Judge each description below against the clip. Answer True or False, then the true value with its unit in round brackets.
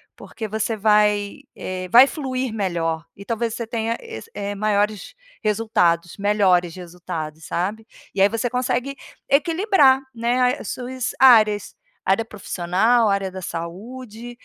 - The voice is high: True (215 Hz)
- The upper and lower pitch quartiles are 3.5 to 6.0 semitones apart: True (4.4 semitones)